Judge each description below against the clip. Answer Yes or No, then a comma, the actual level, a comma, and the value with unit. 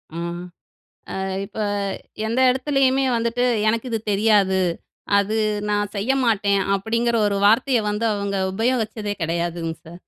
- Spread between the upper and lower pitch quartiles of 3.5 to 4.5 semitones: No, average, 2.8 semitones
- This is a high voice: Yes, high, 215 Hz